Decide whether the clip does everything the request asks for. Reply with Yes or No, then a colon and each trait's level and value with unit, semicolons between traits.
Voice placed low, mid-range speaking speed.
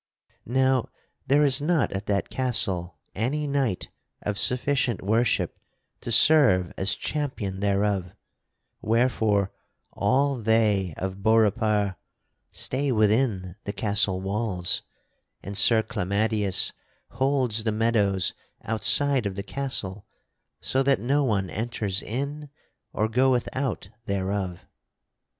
No: low, 110 Hz; slow, 110 wpm